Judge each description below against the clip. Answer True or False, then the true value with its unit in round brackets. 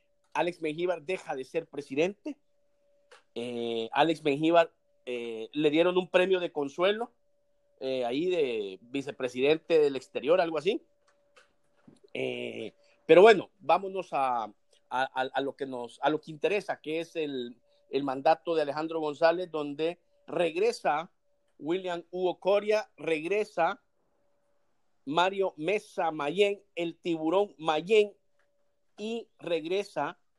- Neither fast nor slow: False (120 wpm)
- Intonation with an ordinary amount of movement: False (6.2 semitones)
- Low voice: False (175 Hz)